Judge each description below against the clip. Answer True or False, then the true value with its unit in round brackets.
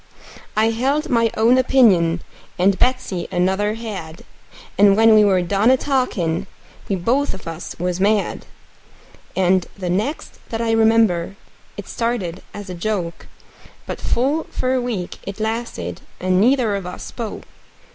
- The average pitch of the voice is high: True (210 Hz)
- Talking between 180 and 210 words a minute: False (150 wpm)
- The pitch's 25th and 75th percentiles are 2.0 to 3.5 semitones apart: False (4.5 semitones)